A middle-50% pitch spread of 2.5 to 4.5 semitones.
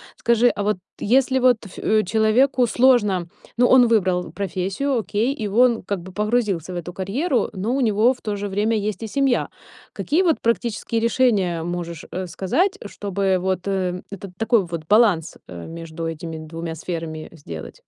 No: average, 5.0 semitones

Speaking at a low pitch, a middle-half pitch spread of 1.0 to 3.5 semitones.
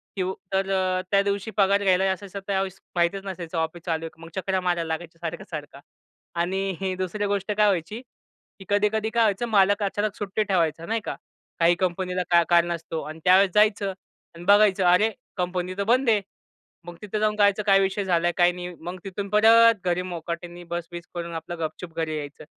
No: medium, 185 Hz; average, 2.9 semitones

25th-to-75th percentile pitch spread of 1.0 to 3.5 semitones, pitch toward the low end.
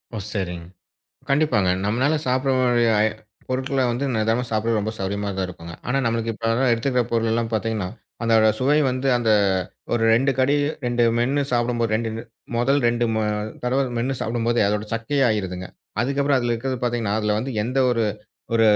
Yes: average, 2.9 semitones; low, 120 Hz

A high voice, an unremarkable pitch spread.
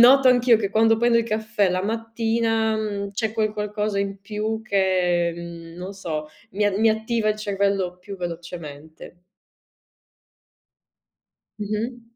Yes: high, 210 Hz; average, 3.1 semitones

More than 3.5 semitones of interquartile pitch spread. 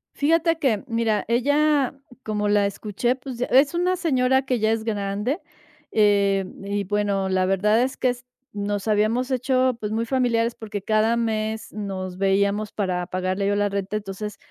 Yes: average, 3.9 semitones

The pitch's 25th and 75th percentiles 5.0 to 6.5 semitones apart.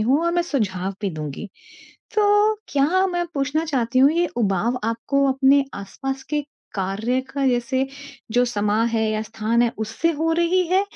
Yes: average, 5.3 semitones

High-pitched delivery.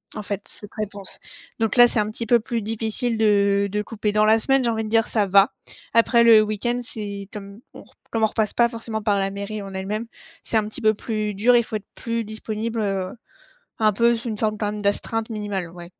Yes: high, 215 Hz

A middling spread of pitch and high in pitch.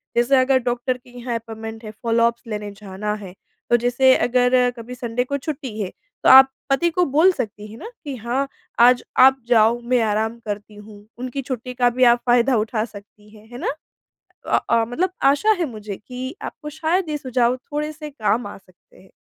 Yes: average, 3.2 semitones; high, 245 Hz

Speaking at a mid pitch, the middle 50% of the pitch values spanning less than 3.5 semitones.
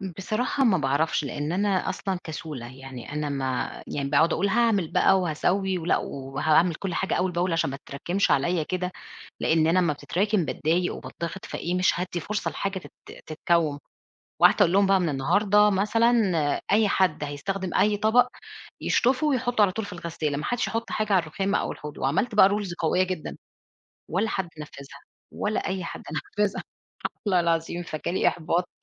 No: medium, 180 Hz; average, 4.2 semitones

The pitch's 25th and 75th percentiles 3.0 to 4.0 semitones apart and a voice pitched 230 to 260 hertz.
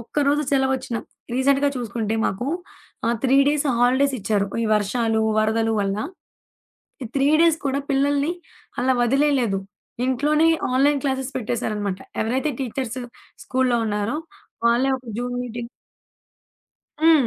Yes: average, 3.6 semitones; very high, 255 Hz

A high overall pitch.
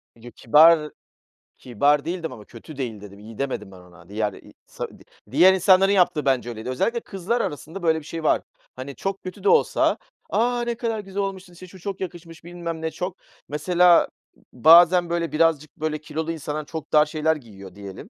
No: medium, 160 Hz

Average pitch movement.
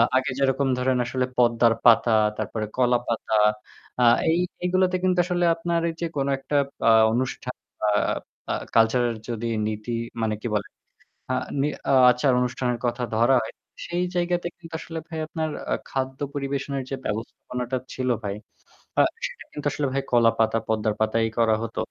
Yes: average, 4.0 semitones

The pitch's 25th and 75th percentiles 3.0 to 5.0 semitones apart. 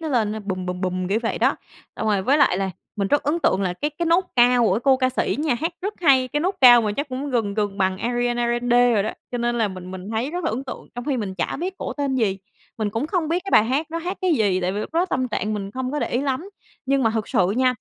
No: wide, 5.6 semitones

